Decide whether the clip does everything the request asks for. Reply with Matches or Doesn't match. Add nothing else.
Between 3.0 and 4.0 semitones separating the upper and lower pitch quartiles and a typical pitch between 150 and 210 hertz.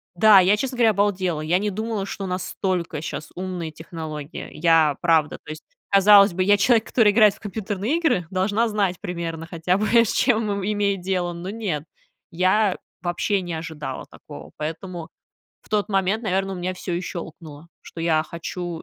Matches